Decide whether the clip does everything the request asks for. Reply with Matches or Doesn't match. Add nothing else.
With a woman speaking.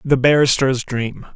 Doesn't match